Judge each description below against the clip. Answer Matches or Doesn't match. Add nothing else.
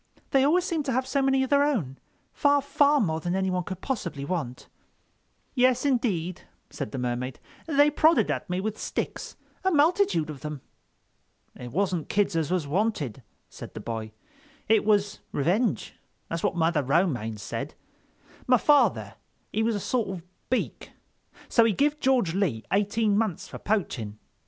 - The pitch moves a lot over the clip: Matches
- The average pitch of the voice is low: Doesn't match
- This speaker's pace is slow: Doesn't match